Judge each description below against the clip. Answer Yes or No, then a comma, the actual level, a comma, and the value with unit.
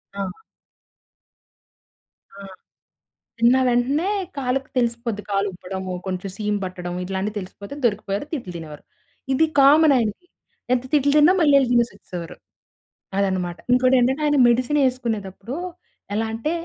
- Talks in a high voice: Yes, high, 235 Hz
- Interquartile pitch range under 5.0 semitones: No, average, 5.3 semitones